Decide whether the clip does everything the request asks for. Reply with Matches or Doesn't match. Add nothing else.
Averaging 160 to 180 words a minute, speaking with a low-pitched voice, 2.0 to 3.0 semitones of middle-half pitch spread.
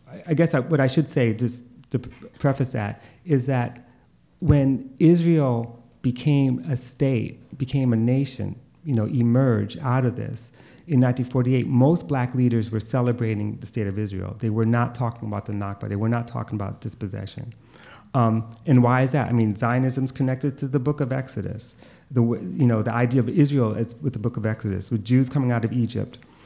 Doesn't match